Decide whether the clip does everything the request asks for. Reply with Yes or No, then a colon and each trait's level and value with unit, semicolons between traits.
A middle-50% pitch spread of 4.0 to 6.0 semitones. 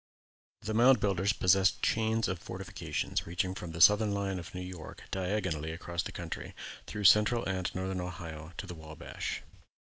No: average, 3.0 semitones